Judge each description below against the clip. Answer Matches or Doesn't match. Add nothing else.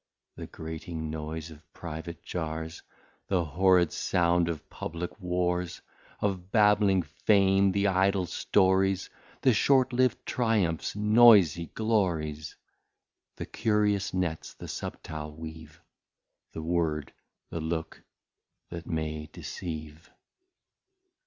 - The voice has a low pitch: Matches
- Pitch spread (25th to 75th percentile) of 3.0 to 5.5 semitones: Matches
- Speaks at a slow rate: Matches